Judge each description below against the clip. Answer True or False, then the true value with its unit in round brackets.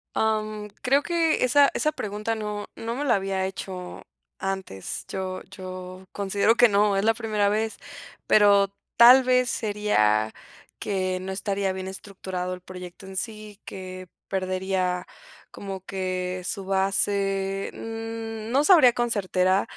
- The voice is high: True (200 Hz)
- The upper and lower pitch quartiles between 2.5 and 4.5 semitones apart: True (2.9 semitones)